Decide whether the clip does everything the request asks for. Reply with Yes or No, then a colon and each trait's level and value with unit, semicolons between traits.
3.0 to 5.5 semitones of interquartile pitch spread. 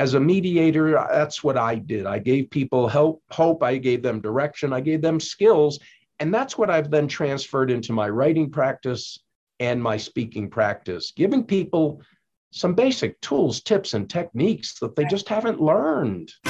Yes: average, 4.7 semitones